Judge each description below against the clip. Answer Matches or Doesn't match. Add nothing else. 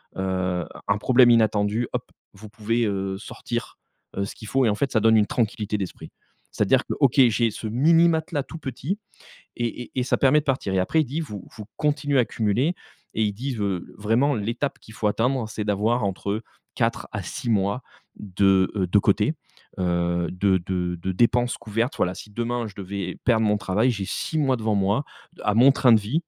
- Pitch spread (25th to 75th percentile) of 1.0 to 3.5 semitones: Doesn't match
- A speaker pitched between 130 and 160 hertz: Doesn't match